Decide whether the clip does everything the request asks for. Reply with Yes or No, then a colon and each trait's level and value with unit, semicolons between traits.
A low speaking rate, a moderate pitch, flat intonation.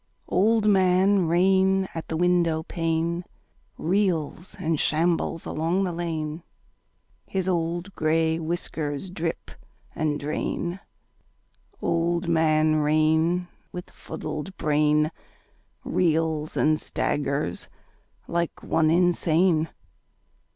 Yes: slow, 90 wpm; medium, 165 Hz; narrow, 2.3 semitones